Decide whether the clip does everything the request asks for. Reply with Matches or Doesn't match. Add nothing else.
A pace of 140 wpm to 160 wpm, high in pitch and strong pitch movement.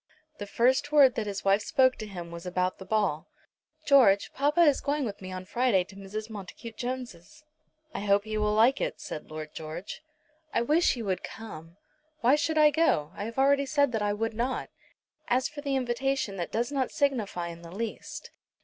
Doesn't match